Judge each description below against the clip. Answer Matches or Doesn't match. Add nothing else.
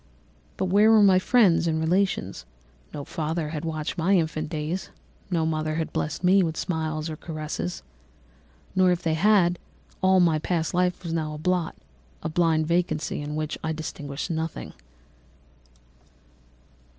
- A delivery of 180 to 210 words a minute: Doesn't match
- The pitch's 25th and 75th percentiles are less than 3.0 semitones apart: Matches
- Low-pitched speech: Doesn't match